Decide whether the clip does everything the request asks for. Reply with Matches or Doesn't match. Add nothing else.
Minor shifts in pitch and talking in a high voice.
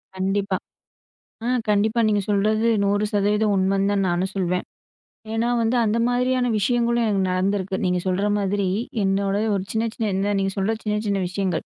Matches